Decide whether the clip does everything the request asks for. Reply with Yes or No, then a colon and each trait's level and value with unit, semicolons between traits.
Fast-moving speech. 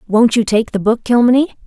Yes: fast, 215 wpm